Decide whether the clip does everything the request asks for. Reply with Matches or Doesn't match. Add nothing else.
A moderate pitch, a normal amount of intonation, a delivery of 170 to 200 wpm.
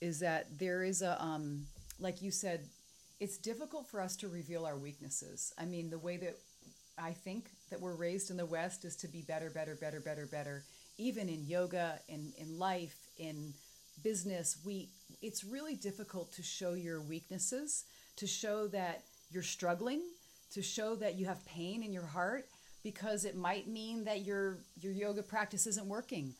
Matches